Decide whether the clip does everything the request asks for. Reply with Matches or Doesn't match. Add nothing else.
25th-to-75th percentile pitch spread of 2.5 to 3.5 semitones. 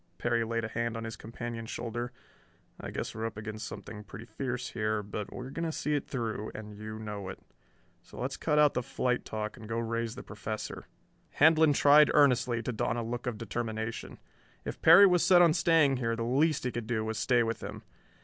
Matches